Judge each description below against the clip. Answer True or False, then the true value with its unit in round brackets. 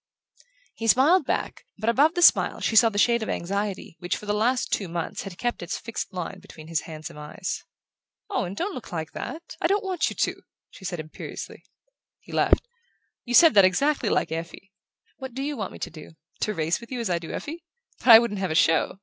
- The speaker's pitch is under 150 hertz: False (210 Hz)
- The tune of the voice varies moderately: False (6.8 semitones)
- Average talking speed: False (220 wpm)